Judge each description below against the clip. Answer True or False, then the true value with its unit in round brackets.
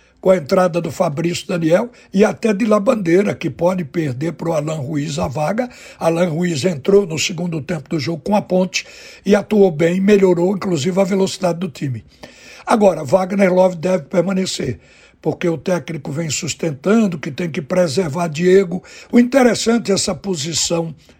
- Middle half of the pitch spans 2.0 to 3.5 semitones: True (2.8 semitones)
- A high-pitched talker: False (180 Hz)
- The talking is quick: False (170 wpm)